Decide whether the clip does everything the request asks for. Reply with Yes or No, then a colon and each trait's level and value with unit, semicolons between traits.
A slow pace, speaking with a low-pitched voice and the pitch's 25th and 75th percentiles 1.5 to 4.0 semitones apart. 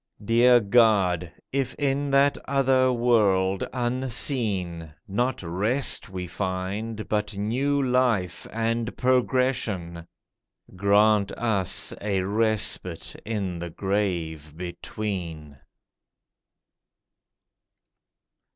No: slow, 80 wpm; low, 105 Hz; average, 5.0 semitones